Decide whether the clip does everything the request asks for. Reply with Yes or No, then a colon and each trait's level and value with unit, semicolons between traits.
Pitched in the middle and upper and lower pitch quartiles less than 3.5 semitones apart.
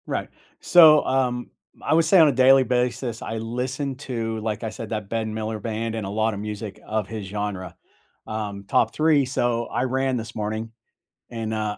No: low, 115 Hz; average, 2.9 semitones